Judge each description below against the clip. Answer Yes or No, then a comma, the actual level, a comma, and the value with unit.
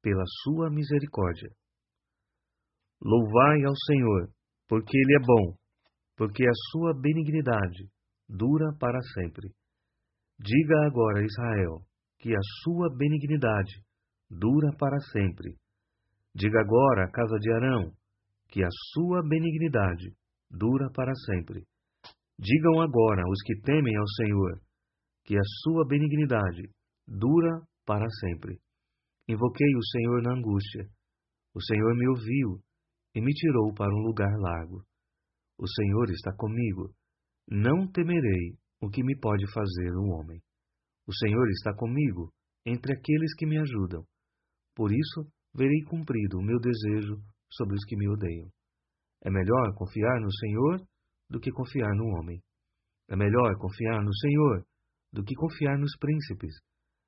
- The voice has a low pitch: Yes, low, 110 Hz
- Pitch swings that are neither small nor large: No, wide, 5.7 semitones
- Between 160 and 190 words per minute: No, average, 130 wpm